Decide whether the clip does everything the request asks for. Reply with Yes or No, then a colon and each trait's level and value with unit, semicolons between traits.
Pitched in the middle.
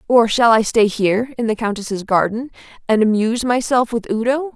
No: high, 230 Hz